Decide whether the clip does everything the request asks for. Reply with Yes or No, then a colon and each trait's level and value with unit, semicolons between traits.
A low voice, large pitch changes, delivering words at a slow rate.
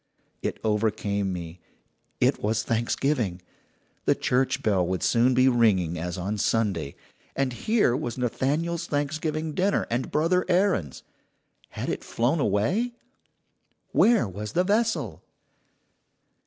Yes: low, 120 Hz; wide, 7.4 semitones; slow, 120 wpm